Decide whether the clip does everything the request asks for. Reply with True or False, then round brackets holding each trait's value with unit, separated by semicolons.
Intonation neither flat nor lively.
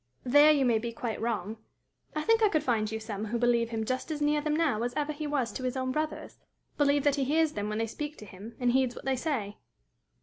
True (4.6 semitones)